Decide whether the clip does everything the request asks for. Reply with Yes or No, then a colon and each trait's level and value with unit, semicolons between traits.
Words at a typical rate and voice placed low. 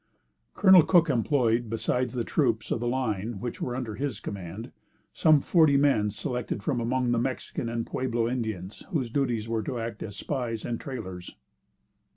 Yes: average, 170 wpm; low, 120 Hz